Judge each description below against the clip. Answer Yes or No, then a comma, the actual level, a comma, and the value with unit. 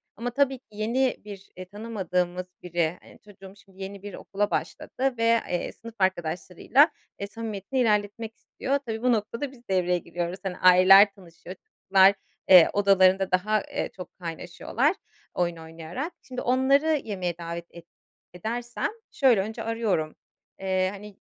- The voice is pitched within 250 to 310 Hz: No, high, 200 Hz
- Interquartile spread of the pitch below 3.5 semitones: No, average, 4.1 semitones